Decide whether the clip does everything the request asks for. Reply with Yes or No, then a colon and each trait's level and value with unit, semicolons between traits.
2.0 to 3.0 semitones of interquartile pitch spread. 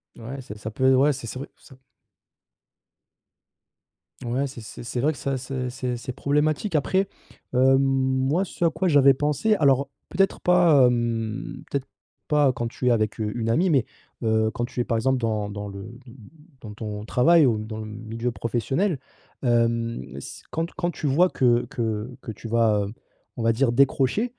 No: average, 3.6 semitones